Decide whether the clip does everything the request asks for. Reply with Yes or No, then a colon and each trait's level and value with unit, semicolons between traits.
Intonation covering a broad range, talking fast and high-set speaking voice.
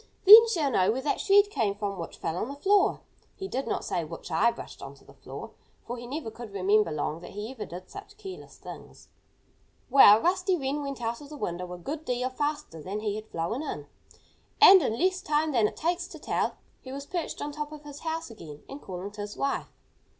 Yes: wide, 7.3 semitones; fast, 230 wpm; very high, 260 Hz